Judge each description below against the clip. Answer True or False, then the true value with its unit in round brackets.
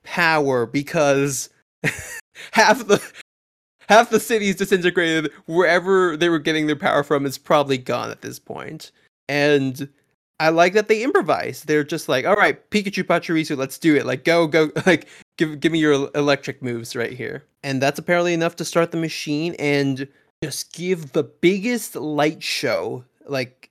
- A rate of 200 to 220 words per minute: False (165 wpm)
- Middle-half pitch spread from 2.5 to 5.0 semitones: True (3.8 semitones)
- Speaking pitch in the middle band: True (160 Hz)